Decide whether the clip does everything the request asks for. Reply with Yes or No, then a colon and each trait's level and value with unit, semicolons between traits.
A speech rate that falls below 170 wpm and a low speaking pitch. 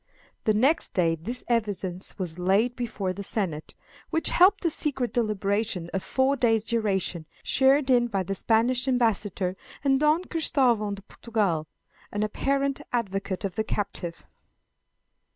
No: average, 140 wpm; high, 220 Hz